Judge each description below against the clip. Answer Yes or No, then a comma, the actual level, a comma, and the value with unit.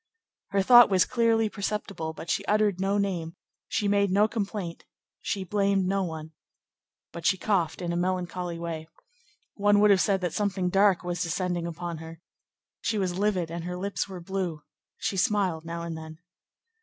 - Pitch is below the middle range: No, medium, 185 Hz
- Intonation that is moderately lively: Yes, average, 3.0 semitones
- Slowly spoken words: No, average, 175 wpm